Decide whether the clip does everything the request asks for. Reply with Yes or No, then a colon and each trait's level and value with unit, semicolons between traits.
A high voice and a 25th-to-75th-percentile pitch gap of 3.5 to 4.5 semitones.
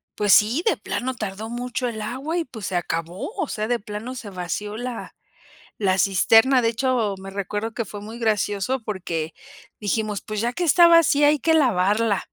Yes: high, 220 Hz; average, 3.9 semitones